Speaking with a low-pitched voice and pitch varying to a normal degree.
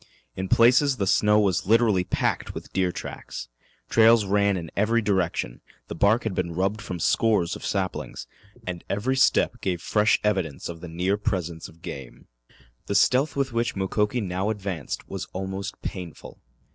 Yes: low, 100 Hz; average, 3.3 semitones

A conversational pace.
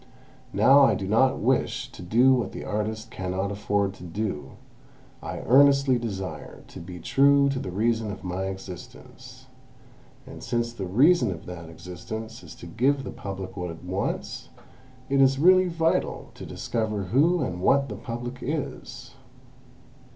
Yes: average, 160 wpm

